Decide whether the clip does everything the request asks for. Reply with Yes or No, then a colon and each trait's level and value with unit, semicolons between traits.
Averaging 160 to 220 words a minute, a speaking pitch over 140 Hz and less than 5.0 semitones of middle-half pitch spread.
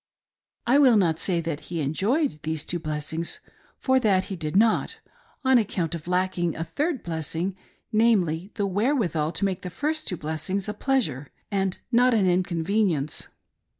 No: average, 165 wpm; medium, 185 Hz; average, 5.3 semitones